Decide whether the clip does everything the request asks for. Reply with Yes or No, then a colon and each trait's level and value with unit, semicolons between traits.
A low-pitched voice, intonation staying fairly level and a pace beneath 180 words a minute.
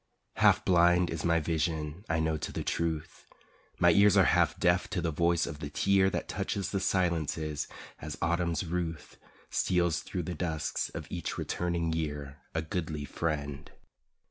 Yes: very low, 85 Hz; narrow, 2.3 semitones; average, 165 wpm